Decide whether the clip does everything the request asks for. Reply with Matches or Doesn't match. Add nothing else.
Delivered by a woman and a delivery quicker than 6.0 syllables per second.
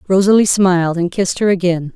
Matches